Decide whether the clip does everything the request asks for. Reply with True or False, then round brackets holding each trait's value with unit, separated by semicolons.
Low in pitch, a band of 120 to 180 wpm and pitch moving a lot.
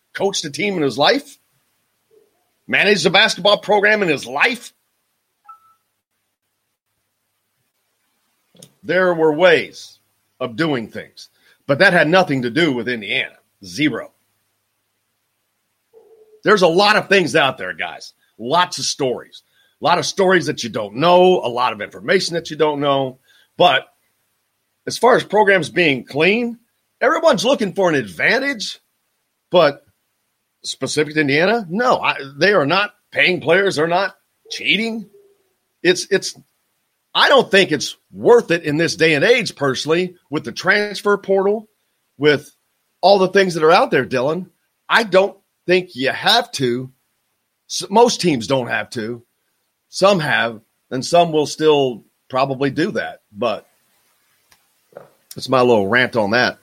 False (165 Hz; 145 wpm; 7.2 semitones)